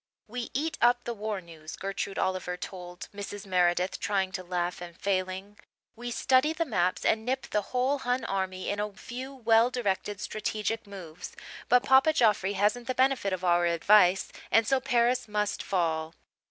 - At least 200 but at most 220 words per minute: No, average, 170 wpm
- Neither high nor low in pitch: No, high, 205 Hz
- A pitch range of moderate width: Yes, average, 4.7 semitones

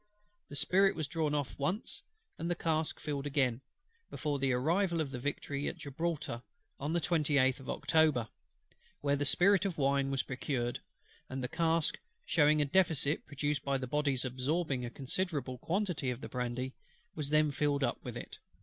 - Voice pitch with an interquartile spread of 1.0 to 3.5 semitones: Yes, average, 3.2 semitones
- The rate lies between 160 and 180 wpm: Yes, average, 170 wpm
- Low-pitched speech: No, medium, 145 Hz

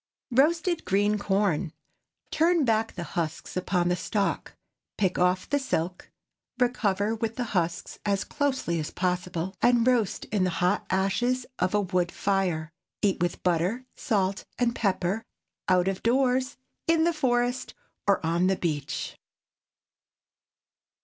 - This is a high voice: Yes, high, 195 Hz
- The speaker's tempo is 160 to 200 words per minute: No, slow, 135 wpm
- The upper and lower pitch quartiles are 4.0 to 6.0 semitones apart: Yes, average, 5.2 semitones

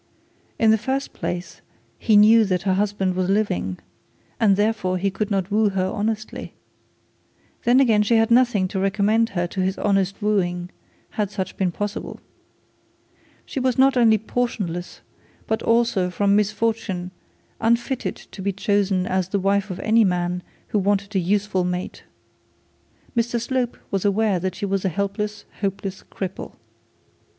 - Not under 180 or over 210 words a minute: No, average, 155 wpm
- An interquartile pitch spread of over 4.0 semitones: No, average, 2.8 semitones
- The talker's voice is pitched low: No, high, 200 Hz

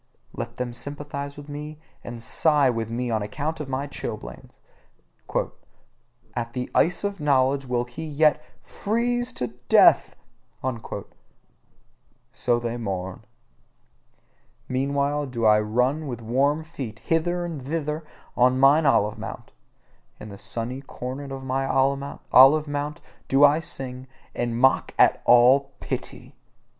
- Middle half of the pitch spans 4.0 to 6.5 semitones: No, average, 3.5 semitones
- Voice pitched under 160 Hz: Yes, low, 135 Hz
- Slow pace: Yes, slow, 130 wpm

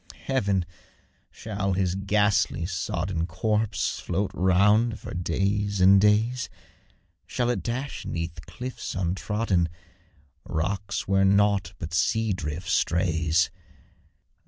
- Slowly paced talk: Yes, slow, 105 wpm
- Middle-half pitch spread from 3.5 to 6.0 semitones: No, average, 3.0 semitones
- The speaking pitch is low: Yes, very low, 95 Hz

